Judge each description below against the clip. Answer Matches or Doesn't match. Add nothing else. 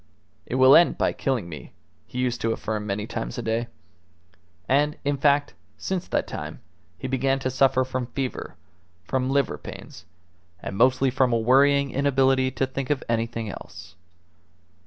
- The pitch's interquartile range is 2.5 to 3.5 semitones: Matches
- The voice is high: Doesn't match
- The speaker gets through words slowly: Doesn't match